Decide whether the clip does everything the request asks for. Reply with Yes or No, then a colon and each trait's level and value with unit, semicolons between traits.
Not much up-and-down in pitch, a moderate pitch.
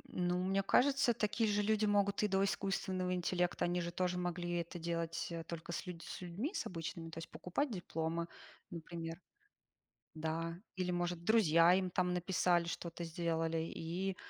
Yes: narrow, 2.3 semitones; medium, 175 Hz